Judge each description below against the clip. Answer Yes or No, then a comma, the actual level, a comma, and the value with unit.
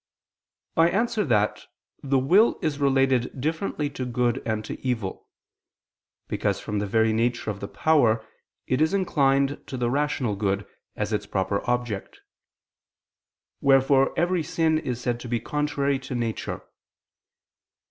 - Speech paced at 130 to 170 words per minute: Yes, average, 140 wpm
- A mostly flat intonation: No, average, 4.6 semitones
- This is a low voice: Yes, low, 130 Hz